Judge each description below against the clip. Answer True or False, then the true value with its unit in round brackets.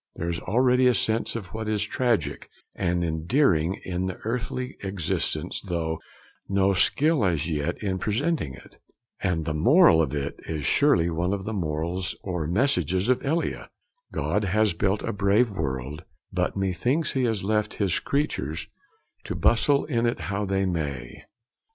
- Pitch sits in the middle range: False (95 Hz)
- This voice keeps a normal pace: True (155 wpm)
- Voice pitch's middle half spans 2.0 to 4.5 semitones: False (5.5 semitones)